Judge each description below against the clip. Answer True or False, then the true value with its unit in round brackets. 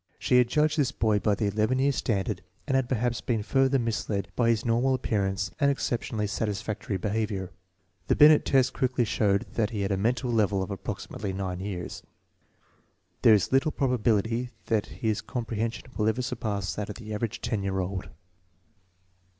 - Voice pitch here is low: True (110 Hz)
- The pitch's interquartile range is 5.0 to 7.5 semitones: False (3.6 semitones)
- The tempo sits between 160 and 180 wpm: True (175 wpm)